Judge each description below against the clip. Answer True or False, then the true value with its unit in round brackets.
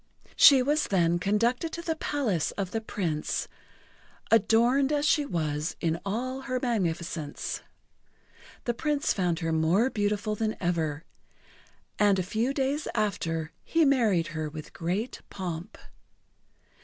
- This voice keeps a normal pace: False (130 wpm)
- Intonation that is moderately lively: False (7.3 semitones)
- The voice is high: True (205 Hz)